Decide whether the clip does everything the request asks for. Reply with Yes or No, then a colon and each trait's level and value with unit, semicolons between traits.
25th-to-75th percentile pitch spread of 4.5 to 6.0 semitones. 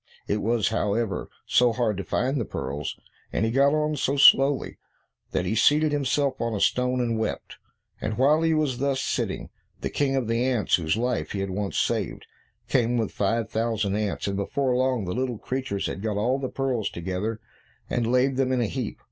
No: average, 4.0 semitones